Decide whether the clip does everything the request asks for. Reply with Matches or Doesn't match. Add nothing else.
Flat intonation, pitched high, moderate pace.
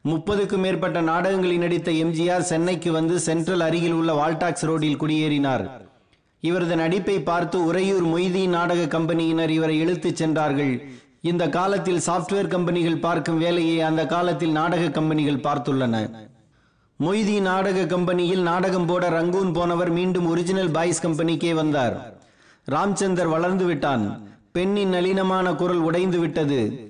Doesn't match